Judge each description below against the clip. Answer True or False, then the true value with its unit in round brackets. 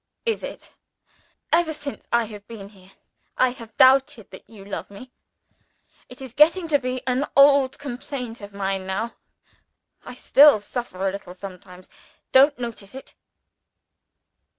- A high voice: True (240 Hz)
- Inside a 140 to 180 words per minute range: True (145 wpm)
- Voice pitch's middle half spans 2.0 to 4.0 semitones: False (5.3 semitones)